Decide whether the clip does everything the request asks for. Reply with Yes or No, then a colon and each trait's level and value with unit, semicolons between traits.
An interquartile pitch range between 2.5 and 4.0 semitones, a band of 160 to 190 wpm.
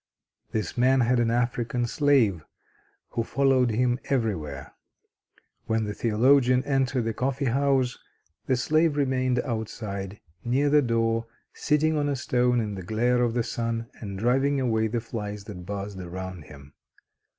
No: average, 3.4 semitones; average, 150 wpm